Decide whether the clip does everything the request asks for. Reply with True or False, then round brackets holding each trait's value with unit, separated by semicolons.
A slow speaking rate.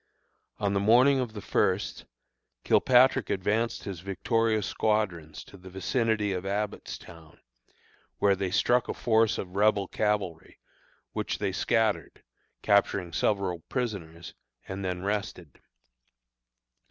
True (115 wpm)